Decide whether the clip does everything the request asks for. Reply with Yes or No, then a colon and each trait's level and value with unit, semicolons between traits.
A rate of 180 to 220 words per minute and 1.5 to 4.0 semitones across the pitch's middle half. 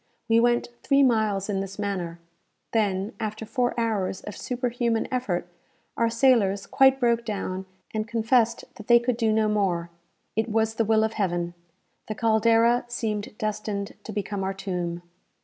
No: average, 160 wpm; average, 2.9 semitones